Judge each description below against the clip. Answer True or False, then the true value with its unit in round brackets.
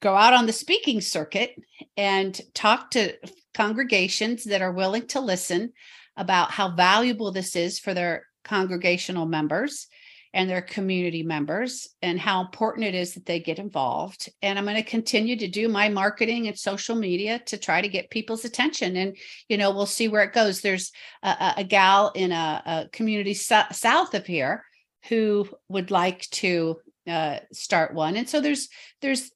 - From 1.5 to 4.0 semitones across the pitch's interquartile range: True (3.7 semitones)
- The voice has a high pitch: True (200 Hz)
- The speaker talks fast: False (175 wpm)